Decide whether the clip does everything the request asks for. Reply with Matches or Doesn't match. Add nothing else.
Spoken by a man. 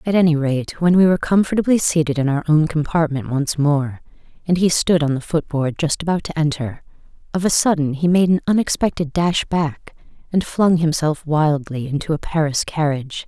Doesn't match